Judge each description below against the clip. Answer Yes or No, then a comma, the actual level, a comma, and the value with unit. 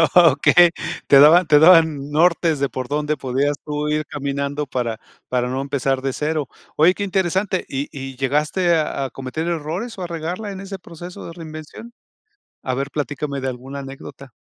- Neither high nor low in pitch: Yes, medium, 150 Hz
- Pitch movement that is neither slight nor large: Yes, average, 3.7 semitones